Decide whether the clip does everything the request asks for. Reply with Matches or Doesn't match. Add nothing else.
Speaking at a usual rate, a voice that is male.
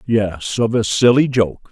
Matches